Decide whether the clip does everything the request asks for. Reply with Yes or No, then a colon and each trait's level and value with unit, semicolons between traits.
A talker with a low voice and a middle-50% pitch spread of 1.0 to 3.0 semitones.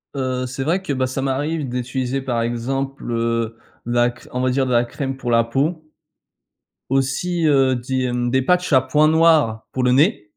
Yes: low, 130 Hz; narrow, 2.6 semitones